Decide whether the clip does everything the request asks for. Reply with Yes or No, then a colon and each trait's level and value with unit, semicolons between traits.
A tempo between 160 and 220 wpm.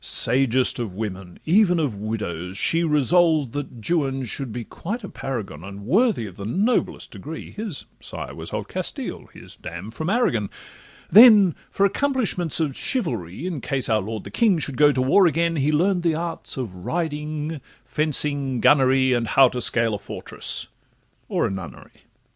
Yes: average, 165 wpm